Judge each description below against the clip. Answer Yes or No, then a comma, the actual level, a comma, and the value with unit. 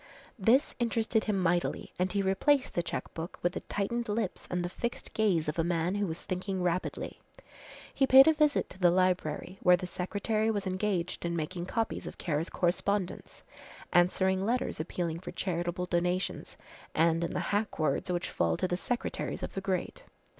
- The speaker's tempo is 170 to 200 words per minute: Yes, average, 180 wpm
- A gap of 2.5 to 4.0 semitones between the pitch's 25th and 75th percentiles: Yes, average, 3.0 semitones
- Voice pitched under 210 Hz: Yes, medium, 185 Hz